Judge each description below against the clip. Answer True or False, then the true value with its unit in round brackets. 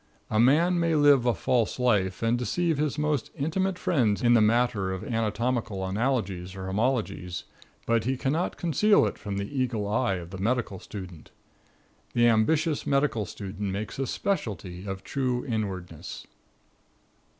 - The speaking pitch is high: False (115 Hz)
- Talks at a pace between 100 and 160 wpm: True (150 wpm)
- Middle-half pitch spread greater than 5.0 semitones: True (5.5 semitones)